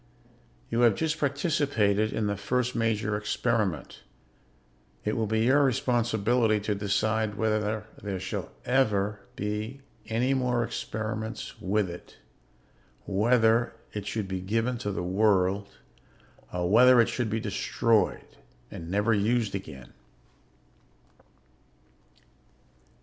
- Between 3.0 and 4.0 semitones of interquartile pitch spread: No, narrow, 2.6 semitones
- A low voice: Yes, low, 110 Hz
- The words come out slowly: Yes, slow, 115 wpm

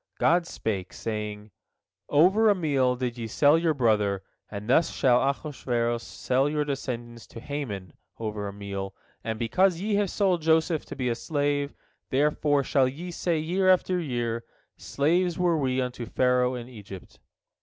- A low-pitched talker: Yes, low, 130 Hz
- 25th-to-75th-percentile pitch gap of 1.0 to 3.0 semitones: No, wide, 5.5 semitones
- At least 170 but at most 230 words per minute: No, average, 160 wpm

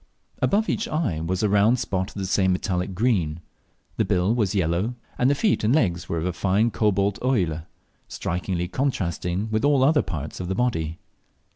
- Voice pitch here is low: Yes, very low, 95 Hz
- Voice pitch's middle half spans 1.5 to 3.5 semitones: No, wide, 5.5 semitones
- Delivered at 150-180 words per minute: No, average, 190 wpm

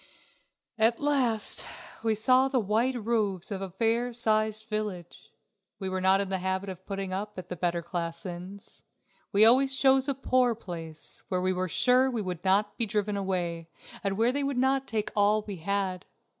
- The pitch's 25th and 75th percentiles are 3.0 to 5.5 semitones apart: Yes, average, 4.0 semitones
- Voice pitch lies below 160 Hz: No, high, 205 Hz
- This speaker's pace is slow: No, average, 185 wpm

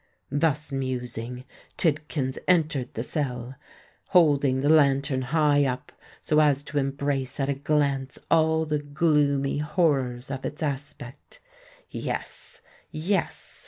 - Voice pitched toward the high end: No, medium, 140 Hz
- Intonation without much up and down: Yes, narrow, 2.3 semitones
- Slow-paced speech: Yes, slow, 115 wpm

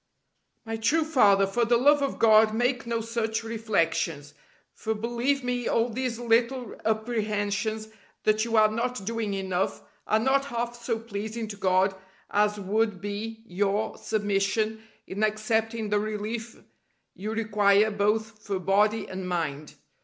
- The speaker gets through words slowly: No, average, 145 wpm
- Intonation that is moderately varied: No, narrow, 2.2 semitones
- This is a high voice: Yes, high, 220 Hz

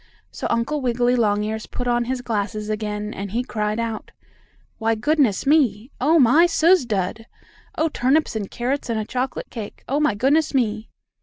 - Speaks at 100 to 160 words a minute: No, average, 170 wpm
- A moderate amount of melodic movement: Yes, average, 4.1 semitones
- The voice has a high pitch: Yes, high, 235 Hz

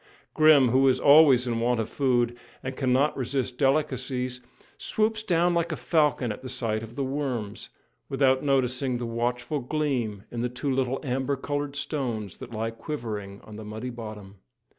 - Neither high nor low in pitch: No, low, 130 Hz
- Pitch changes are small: No, average, 3.2 semitones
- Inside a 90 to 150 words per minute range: No, average, 165 wpm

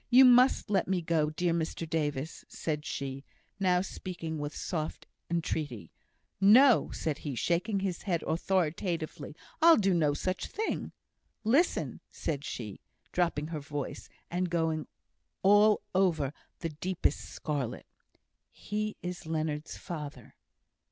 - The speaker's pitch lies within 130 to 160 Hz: No, medium, 170 Hz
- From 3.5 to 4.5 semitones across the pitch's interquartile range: Yes, average, 4.0 semitones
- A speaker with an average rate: No, slow, 125 wpm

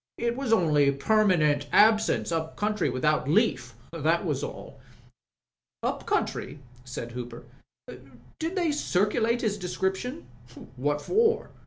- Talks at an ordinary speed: No, slow, 125 wpm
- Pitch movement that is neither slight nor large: No, wide, 7.8 semitones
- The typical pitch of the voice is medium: Yes, medium, 175 Hz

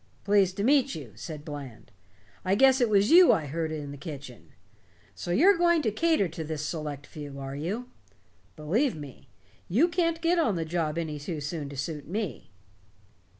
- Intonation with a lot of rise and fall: Yes, wide, 8.4 semitones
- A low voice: No, medium, 165 Hz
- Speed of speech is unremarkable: Yes, average, 185 wpm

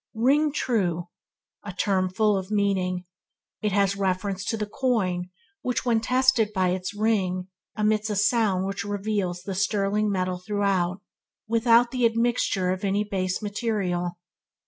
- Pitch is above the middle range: Yes, high, 200 Hz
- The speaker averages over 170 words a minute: No, average, 145 wpm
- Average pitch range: Yes, average, 3.0 semitones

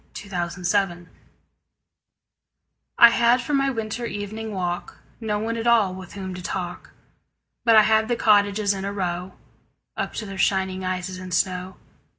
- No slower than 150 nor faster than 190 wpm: Yes, average, 160 wpm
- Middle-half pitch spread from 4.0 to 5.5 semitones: No, average, 3.1 semitones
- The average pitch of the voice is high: Yes, high, 200 Hz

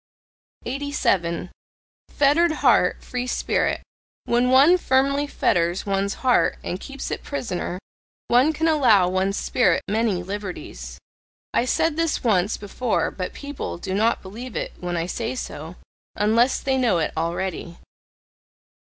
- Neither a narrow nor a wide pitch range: No, wide, 6.5 semitones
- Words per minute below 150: Yes, slow, 135 wpm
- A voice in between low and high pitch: No, high, 225 Hz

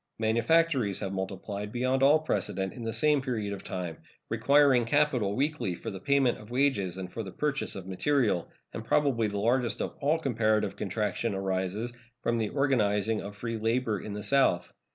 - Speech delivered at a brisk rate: No, average, 175 wpm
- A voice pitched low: Yes, low, 115 Hz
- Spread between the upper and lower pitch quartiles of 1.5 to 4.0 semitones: No, average, 5.0 semitones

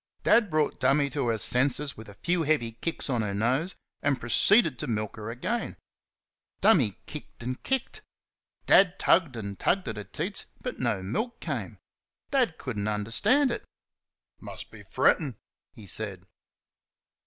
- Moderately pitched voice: No, low, 130 Hz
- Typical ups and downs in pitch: No, wide, 7.2 semitones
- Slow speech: No, average, 155 wpm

